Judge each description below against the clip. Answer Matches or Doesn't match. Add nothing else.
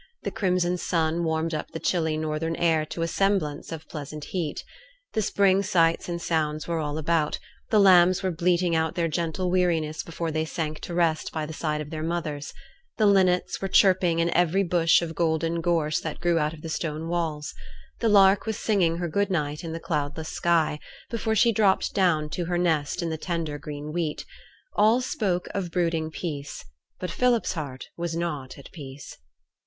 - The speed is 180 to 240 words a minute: Matches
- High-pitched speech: Doesn't match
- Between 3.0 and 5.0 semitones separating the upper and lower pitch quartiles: Doesn't match